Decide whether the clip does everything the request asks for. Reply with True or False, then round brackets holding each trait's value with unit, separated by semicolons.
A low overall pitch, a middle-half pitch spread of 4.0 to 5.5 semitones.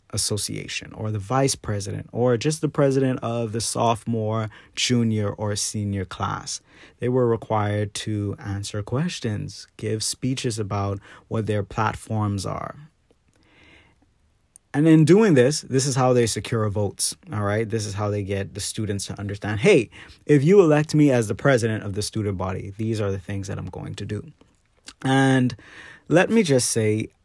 True (110 Hz; 4.4 semitones)